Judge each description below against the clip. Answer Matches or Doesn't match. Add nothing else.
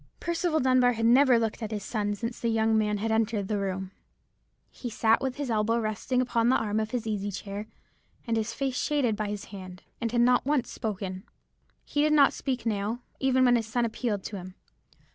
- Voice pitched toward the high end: Matches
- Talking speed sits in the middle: Doesn't match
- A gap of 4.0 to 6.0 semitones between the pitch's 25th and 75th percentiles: Doesn't match